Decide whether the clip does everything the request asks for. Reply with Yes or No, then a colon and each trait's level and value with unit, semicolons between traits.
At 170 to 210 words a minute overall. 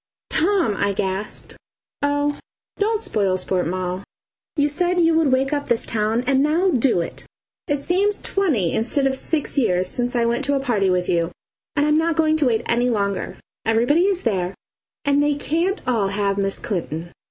Yes: average, 185 wpm